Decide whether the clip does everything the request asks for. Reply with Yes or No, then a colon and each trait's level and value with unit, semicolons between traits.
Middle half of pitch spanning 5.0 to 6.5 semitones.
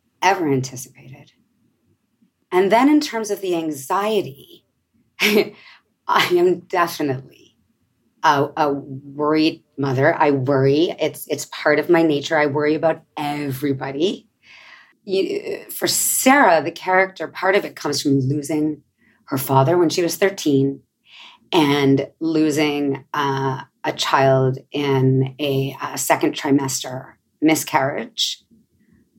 No: average, 3.5 semitones